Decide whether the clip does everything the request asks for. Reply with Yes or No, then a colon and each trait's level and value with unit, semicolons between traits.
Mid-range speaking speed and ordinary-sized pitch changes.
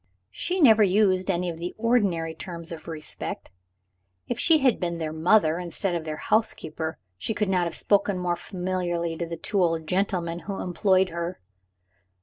Yes: average, 170 wpm; average, 3.0 semitones